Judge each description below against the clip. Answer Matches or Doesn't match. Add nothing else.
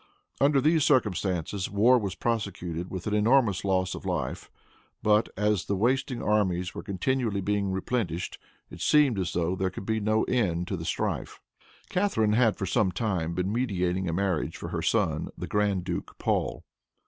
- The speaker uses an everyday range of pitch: Matches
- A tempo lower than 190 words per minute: Matches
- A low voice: Matches